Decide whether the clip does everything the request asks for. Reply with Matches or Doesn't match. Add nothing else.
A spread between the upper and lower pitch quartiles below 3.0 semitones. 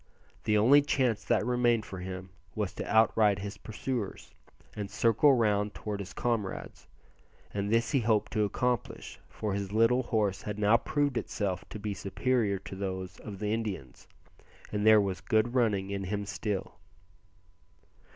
Matches